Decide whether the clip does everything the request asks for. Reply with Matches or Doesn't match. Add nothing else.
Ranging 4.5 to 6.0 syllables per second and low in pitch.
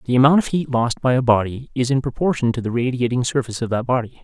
Doesn't match